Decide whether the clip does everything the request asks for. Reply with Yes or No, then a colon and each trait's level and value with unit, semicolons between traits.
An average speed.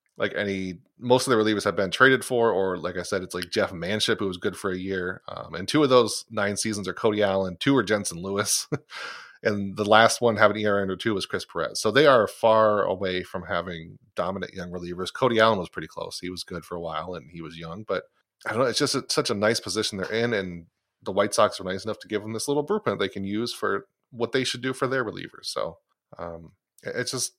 No: fast, 250 wpm